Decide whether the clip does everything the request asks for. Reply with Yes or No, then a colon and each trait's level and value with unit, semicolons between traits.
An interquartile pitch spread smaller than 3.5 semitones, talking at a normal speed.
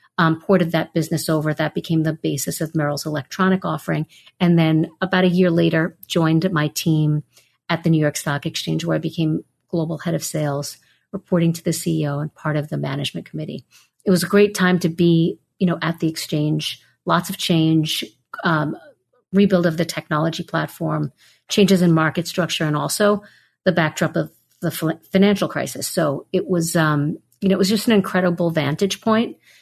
Yes: average, 2.9 semitones; average, 185 wpm